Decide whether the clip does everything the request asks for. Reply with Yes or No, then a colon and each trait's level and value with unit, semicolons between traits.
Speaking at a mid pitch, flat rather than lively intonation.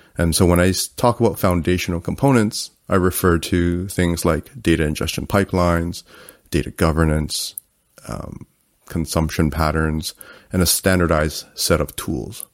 No: very low, 85 Hz; narrow, 2.2 semitones